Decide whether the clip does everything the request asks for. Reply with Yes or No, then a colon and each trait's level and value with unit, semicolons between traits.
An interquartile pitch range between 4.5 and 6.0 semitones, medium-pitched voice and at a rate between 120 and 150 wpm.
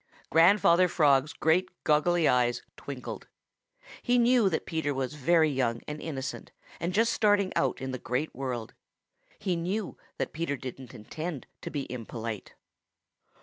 Yes: average, 5.2 semitones; medium, 150 Hz; average, 145 wpm